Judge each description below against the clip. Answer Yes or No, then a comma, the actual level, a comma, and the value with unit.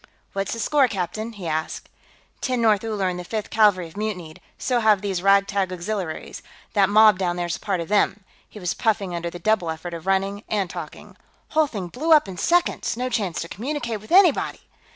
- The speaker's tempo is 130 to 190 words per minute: No, fast, 205 wpm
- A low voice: No, high, 200 Hz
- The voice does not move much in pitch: No, average, 3.7 semitones